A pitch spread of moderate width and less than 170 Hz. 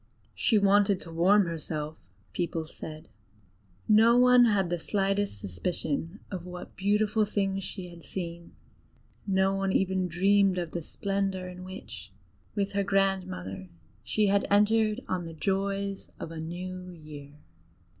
No: average, 3.1 semitones; high, 190 Hz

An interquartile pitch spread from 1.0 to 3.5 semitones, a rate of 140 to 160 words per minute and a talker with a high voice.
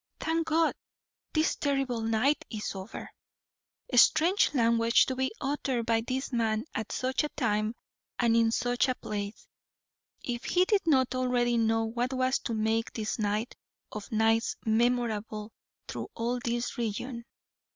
Yes: narrow, 2.6 semitones; average, 145 wpm; high, 235 Hz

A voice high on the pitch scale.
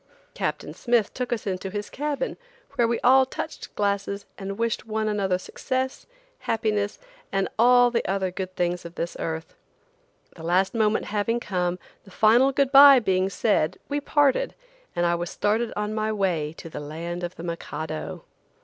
Yes: high, 205 Hz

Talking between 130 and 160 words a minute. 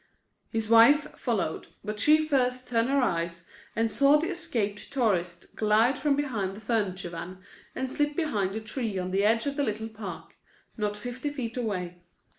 No: average, 175 wpm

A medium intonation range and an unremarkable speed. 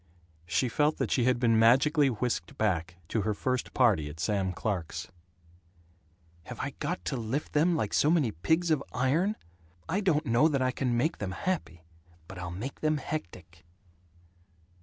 No: wide, 7.7 semitones; average, 170 wpm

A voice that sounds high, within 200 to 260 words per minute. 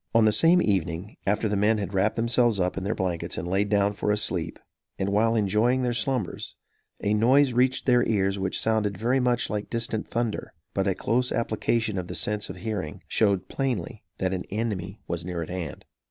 No: low, 105 Hz; fast, 205 wpm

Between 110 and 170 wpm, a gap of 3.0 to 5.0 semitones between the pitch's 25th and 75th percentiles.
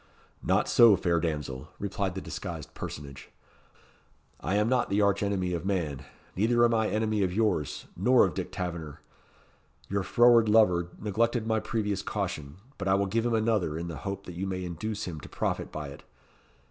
No: average, 185 wpm; average, 4.2 semitones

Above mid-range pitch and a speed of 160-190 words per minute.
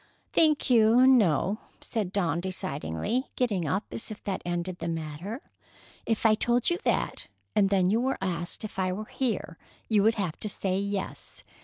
Yes: high, 200 Hz; average, 175 wpm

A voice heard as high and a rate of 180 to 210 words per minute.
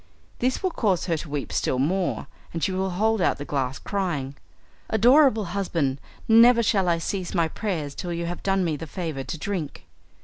No: medium, 180 Hz; average, 195 wpm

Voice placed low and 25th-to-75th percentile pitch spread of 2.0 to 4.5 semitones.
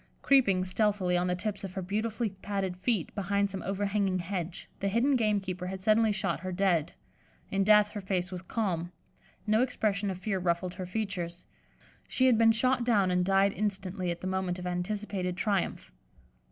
No: high, 195 Hz; narrow, 2.6 semitones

